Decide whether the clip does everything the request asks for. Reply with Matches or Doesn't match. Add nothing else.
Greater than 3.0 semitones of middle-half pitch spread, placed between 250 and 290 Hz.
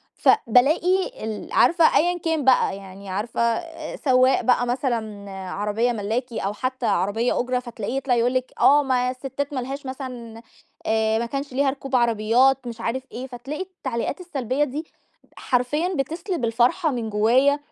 Matches